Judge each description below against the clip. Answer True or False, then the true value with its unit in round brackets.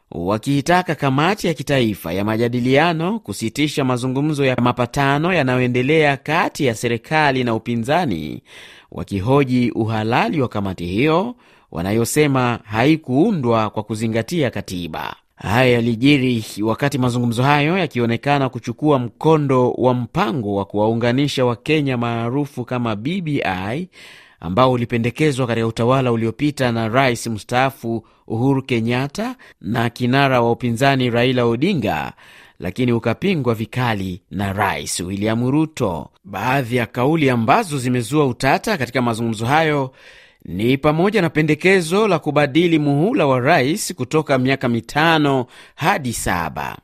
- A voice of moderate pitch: False (125 Hz)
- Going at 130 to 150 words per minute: False (115 wpm)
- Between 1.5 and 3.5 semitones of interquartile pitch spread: False (4.0 semitones)